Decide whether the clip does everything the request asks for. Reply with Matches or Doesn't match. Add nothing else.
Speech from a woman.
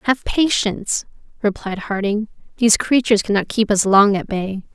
Matches